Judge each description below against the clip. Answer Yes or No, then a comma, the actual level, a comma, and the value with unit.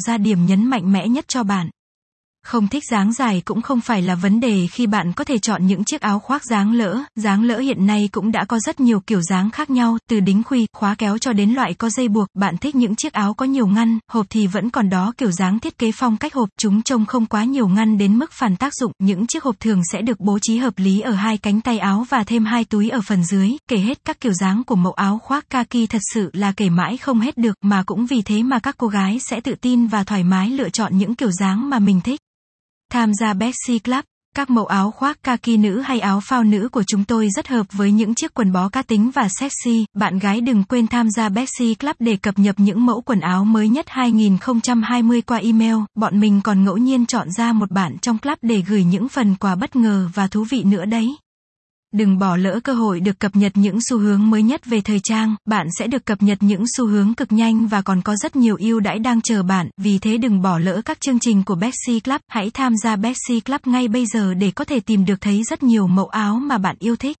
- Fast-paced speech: Yes, fast, 255 wpm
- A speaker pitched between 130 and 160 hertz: No, high, 220 Hz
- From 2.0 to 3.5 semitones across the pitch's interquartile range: Yes, average, 3.1 semitones